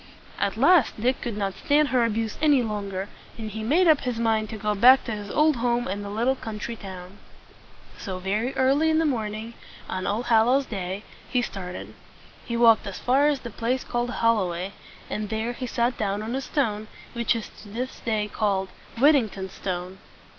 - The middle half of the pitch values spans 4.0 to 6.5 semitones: No, average, 3.5 semitones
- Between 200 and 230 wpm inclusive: Yes, fast, 205 wpm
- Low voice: No, high, 225 Hz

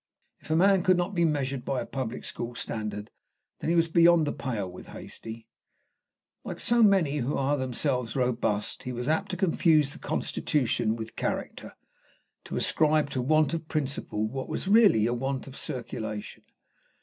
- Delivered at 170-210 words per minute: Yes, average, 175 wpm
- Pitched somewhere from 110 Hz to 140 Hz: Yes, low, 135 Hz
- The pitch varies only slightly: No, wide, 5.5 semitones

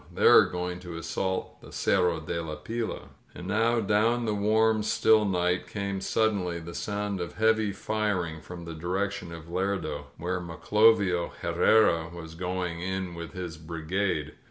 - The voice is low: Yes, very low, 90 Hz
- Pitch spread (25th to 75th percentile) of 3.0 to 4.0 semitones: Yes, average, 3.4 semitones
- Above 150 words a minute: Yes, average, 170 wpm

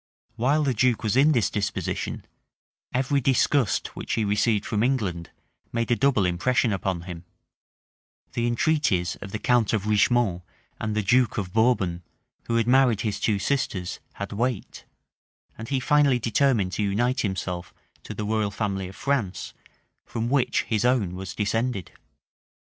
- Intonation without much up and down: No, average, 4.2 semitones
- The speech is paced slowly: No, average, 155 wpm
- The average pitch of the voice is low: Yes, low, 110 Hz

